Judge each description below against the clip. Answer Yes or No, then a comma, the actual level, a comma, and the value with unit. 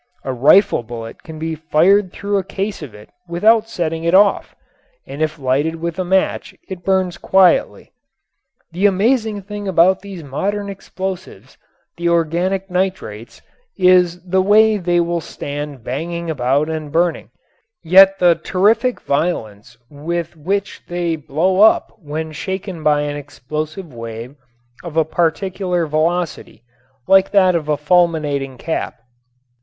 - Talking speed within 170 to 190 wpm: No, average, 140 wpm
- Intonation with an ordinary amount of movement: Yes, average, 3.9 semitones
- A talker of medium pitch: Yes, medium, 170 Hz